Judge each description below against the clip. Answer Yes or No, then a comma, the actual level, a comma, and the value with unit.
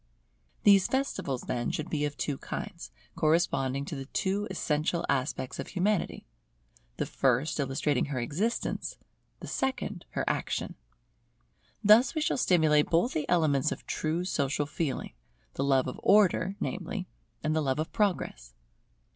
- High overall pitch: No, medium, 155 Hz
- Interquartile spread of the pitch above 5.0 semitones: Yes, wide, 5.5 semitones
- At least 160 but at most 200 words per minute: No, average, 145 wpm